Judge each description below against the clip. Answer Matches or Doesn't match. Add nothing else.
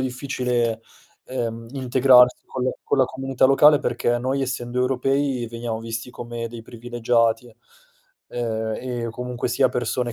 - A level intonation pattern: Matches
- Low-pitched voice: Matches